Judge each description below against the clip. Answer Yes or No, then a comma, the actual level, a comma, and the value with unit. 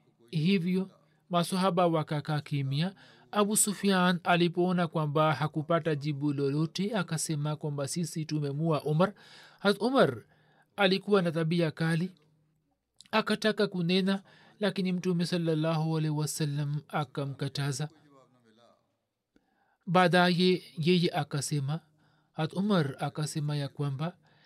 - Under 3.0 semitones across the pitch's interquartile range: No, average, 3.3 semitones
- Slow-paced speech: Yes, slow, 85 wpm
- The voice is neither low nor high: Yes, medium, 160 Hz